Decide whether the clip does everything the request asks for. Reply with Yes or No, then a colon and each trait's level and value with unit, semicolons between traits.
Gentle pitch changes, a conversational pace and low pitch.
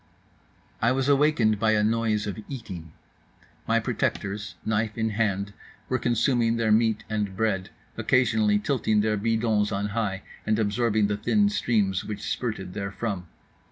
Yes: narrow, 2.0 semitones; average, 145 wpm; low, 110 Hz